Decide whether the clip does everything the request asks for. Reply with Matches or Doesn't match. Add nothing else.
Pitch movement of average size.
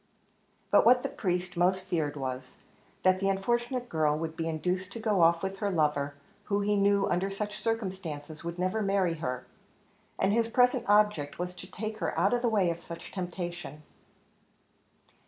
Matches